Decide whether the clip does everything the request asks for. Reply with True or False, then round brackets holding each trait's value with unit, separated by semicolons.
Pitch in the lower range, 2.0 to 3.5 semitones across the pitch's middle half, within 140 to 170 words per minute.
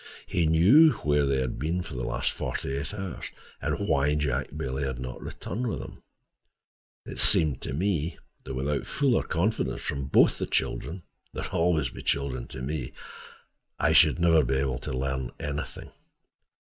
False (75 Hz; 4.2 semitones; 160 wpm)